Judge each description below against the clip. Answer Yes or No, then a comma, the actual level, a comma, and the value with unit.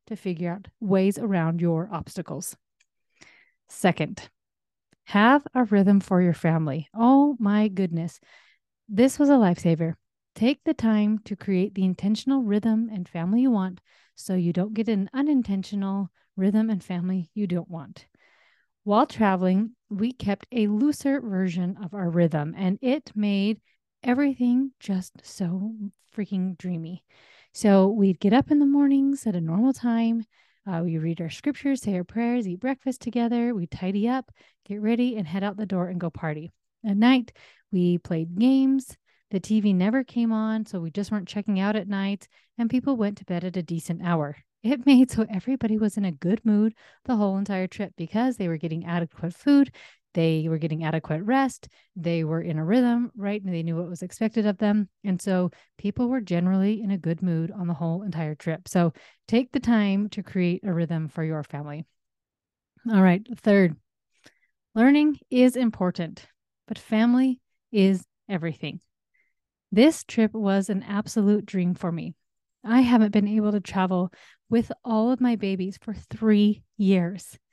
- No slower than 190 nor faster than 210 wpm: No, average, 170 wpm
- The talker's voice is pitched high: Yes, high, 200 Hz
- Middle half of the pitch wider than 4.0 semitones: Yes, average, 4.5 semitones